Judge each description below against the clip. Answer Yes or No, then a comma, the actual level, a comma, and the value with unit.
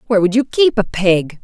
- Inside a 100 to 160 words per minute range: No, fast, 250 wpm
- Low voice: No, high, 205 Hz